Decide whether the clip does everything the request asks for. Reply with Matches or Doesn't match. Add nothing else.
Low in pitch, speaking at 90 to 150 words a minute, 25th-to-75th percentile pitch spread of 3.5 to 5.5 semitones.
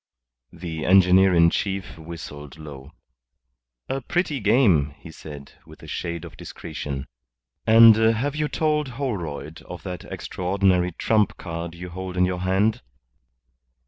Matches